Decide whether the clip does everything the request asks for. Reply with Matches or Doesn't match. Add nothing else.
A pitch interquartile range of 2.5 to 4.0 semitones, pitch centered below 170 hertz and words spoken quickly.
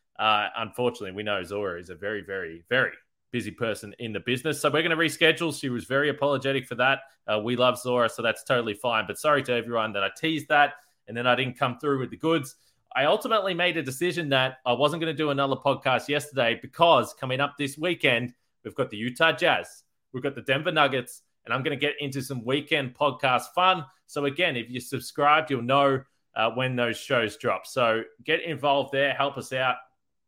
Matches